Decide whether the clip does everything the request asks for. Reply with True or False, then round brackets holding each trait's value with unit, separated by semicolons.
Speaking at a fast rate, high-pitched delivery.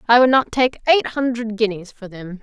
True (225 wpm; 230 Hz)